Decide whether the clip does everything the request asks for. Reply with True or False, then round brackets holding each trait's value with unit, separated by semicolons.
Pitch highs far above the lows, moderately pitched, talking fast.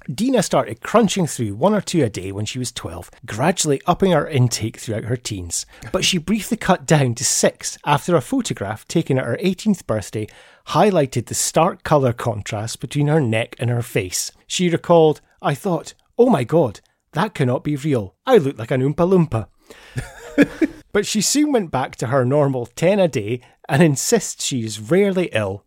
False (7.4 semitones; 145 Hz; 185 wpm)